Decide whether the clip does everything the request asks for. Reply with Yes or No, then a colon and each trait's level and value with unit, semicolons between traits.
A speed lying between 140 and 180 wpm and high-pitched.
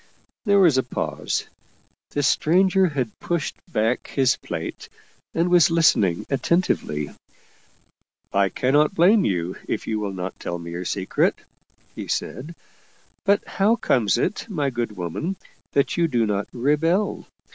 No: average, 145 wpm; low, 135 Hz